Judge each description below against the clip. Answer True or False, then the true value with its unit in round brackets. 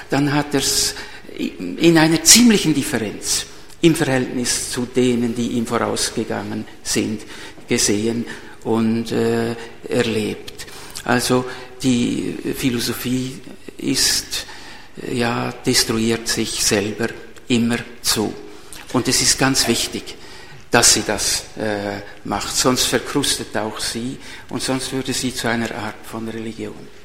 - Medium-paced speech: False (120 wpm)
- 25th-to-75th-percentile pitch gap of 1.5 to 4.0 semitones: True (2.4 semitones)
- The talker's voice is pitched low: True (120 Hz)